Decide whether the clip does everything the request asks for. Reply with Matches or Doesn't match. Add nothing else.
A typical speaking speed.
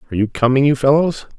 Doesn't match